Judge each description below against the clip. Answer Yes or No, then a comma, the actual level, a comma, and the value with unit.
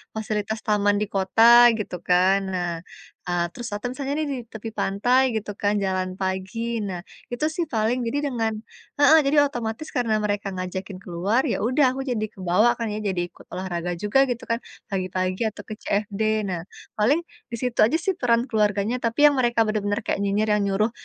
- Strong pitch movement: No, average, 3.7 semitones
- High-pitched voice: Yes, high, 210 Hz